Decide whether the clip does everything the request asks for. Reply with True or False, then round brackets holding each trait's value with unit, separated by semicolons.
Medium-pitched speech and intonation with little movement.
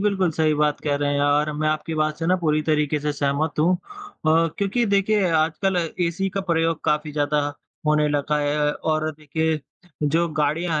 True (155 Hz; 2.2 semitones)